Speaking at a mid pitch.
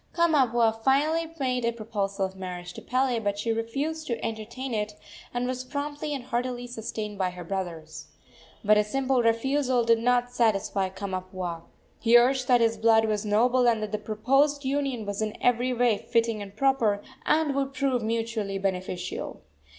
No: high, 230 Hz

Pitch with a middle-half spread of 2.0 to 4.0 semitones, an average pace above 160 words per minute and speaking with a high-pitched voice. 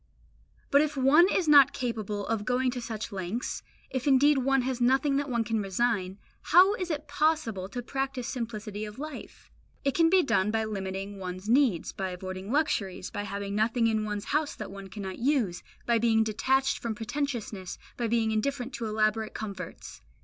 No: average, 4.9 semitones; average, 180 wpm; high, 230 Hz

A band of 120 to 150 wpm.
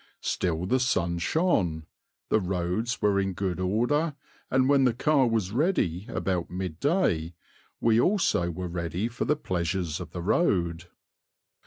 Yes: average, 145 wpm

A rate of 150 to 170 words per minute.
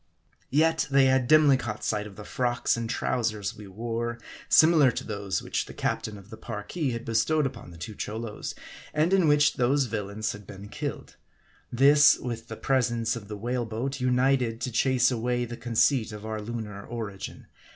No: average, 190 wpm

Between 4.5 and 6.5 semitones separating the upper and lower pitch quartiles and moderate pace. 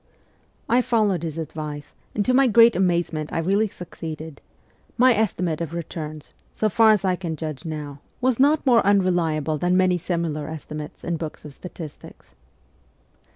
Yes: average, 4.9 semitones; average, 160 wpm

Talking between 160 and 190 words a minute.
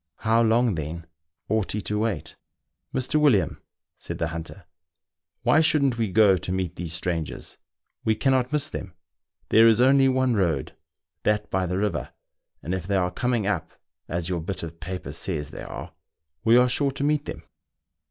Yes: average, 185 wpm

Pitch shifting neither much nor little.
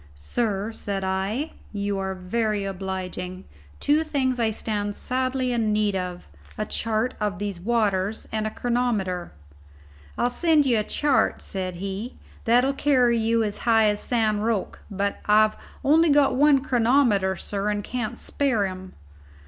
Yes: average, 3.9 semitones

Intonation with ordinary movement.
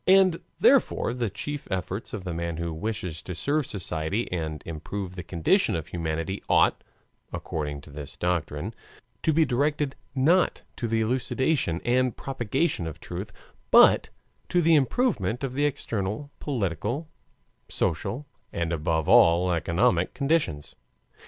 No: wide, 8.4 semitones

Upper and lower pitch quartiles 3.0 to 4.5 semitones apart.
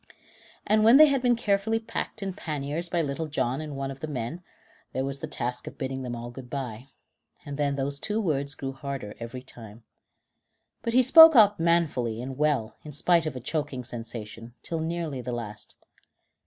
No: wide, 5.4 semitones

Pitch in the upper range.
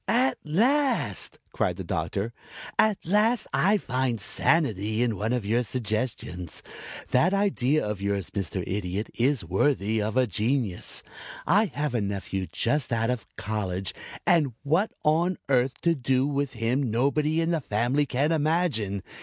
No: low, 125 Hz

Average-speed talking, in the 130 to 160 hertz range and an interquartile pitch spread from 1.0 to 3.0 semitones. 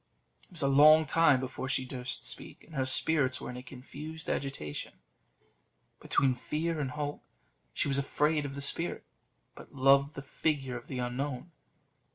Yes: average, 170 wpm; medium, 140 Hz; narrow, 2.6 semitones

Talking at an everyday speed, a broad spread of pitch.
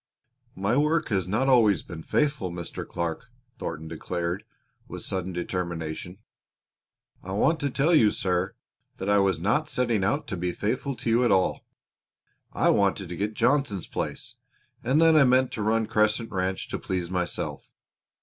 Yes: average, 165 wpm; wide, 5.7 semitones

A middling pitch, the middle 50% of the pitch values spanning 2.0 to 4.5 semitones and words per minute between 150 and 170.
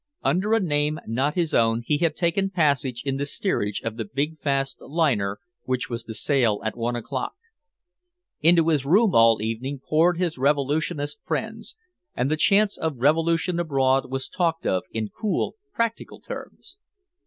No: medium, 145 Hz; average, 5.0 semitones; average, 165 wpm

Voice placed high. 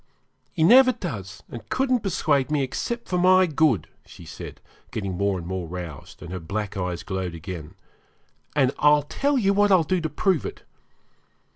No: medium, 140 Hz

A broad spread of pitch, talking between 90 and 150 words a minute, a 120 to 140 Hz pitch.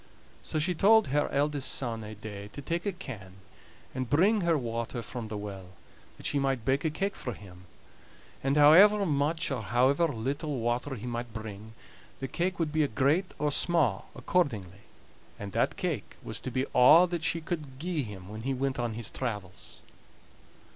No: wide, 6.0 semitones; average, 180 wpm; low, 135 Hz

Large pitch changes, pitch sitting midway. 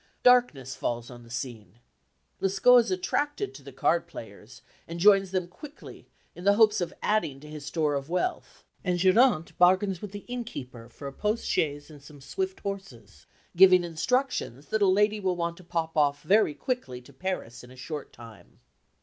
Yes: wide, 6.9 semitones; medium, 175 Hz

